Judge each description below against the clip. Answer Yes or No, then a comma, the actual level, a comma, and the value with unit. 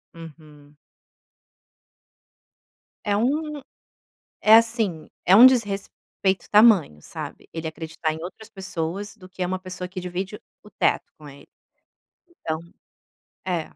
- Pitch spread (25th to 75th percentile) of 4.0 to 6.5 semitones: Yes, average, 4.7 semitones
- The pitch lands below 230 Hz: Yes, medium, 185 Hz